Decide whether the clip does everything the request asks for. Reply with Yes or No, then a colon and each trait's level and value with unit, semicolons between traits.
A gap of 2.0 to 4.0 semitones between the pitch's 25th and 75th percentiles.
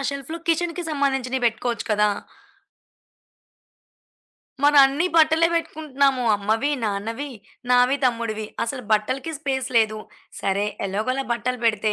No: average, 4.4 semitones